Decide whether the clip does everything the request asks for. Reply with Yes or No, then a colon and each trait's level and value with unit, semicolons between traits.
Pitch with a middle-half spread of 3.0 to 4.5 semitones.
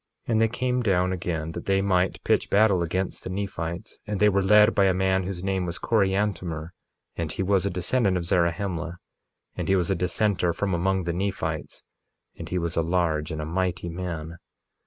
No: narrow, 2.4 semitones